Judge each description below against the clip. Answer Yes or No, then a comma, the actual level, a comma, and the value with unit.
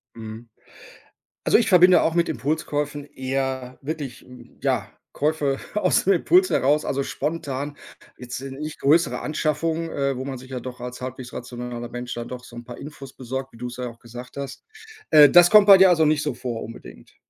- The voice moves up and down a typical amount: Yes, average, 3.7 semitones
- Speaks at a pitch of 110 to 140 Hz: Yes, low, 135 Hz